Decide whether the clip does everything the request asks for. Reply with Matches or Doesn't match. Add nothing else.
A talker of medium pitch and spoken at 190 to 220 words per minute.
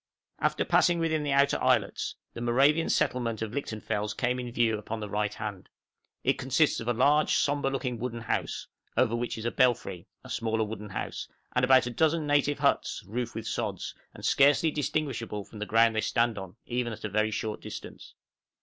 Doesn't match